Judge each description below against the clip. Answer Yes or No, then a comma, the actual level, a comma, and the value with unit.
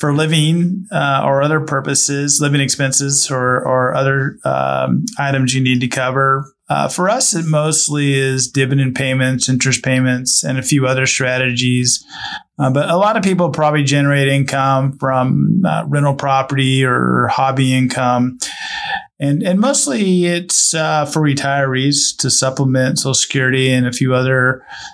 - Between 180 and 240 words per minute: No, average, 150 wpm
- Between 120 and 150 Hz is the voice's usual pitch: Yes, low, 135 Hz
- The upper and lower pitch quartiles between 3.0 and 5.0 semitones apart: No, narrow, 2.5 semitones